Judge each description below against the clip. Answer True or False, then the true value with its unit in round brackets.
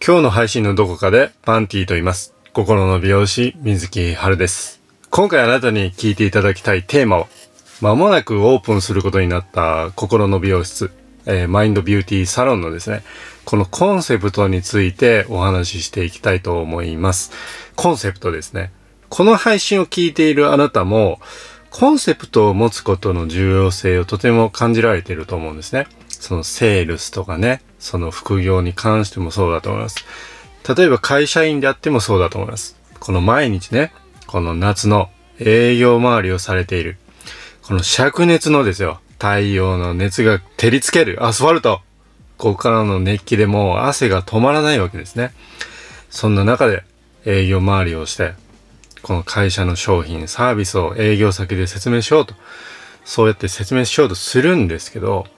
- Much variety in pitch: False (4.1 semitones)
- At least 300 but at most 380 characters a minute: True (360 characters per minute)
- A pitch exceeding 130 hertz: False (100 Hz)